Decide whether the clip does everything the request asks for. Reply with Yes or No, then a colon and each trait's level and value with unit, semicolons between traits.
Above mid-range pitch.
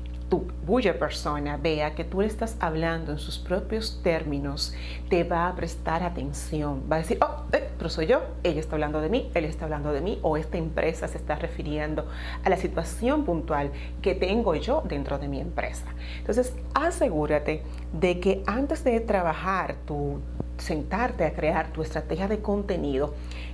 No: medium, 160 Hz